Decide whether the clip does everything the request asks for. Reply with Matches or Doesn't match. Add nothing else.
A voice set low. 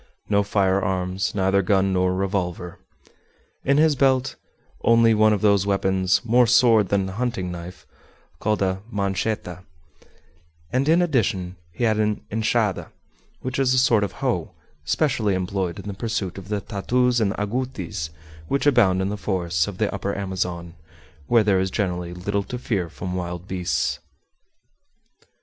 Matches